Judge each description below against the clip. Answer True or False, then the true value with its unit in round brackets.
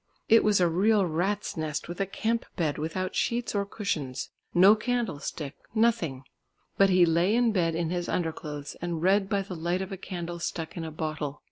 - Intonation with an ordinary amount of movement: True (3.8 semitones)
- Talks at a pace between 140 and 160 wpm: False (200 wpm)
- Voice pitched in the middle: True (175 Hz)